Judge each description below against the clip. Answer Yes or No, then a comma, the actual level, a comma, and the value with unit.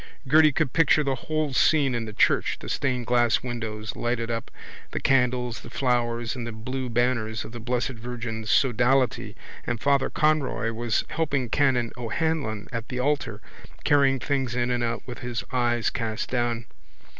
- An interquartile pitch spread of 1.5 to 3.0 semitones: Yes, narrow, 2.4 semitones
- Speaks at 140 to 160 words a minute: No, average, 170 wpm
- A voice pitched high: No, low, 125 Hz